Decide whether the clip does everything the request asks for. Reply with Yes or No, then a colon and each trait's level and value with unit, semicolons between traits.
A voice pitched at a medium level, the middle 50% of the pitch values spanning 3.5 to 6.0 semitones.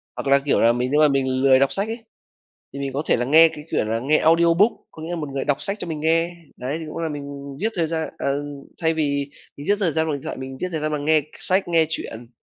No: medium, 150 Hz; average, 3.1 semitones